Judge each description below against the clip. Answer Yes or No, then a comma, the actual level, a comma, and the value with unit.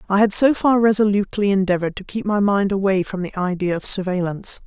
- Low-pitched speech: No, high, 195 Hz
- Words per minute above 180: Yes, fast, 205 wpm